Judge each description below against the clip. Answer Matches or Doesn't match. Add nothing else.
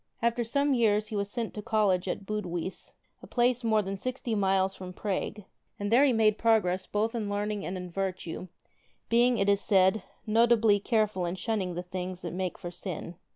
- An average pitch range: Matches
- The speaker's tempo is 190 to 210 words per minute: Matches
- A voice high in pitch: Matches